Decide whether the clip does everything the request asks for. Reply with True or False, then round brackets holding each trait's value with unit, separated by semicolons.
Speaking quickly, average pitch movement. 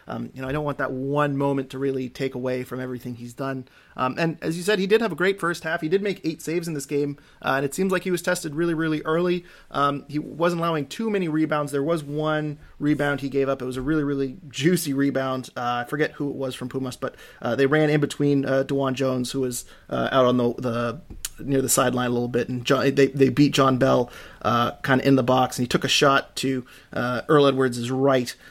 True (255 wpm; 3.0 semitones)